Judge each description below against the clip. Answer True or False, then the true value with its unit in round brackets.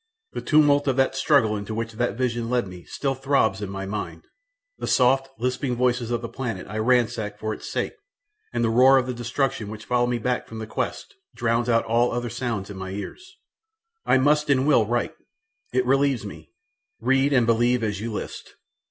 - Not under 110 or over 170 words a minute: False (195 wpm)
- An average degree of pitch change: True (3.1 semitones)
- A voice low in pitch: True (120 Hz)